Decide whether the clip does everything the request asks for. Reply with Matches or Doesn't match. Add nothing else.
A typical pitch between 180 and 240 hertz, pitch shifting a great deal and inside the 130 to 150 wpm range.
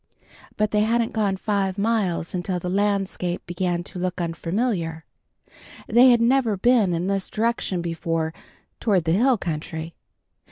Doesn't match